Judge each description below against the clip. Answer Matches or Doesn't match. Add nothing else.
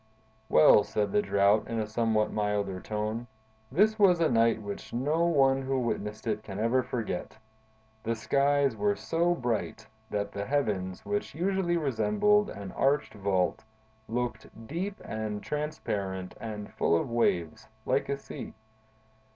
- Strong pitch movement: Matches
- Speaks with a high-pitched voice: Doesn't match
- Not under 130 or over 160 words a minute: Matches